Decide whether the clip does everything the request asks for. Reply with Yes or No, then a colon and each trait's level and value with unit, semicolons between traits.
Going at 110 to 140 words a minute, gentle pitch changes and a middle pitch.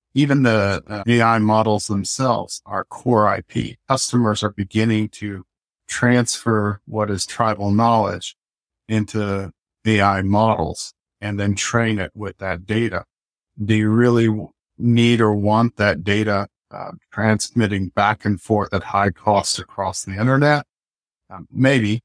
No: slow, 135 wpm; narrow, 2.3 semitones; low, 105 Hz